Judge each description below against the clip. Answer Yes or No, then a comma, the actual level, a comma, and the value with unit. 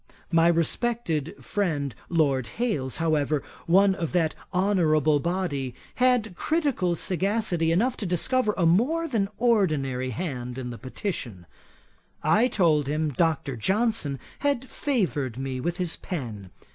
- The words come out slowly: Yes, slow, 130 wpm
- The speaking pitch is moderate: Yes, medium, 170 Hz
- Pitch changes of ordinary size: No, wide, 6.6 semitones